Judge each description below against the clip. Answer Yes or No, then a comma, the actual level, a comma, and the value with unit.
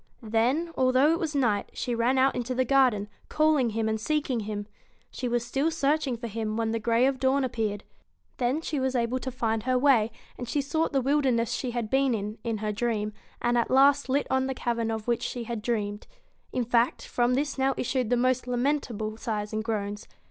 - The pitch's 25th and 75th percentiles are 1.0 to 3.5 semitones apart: Yes, average, 3.0 semitones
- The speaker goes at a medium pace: No, fast, 215 wpm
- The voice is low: No, high, 245 Hz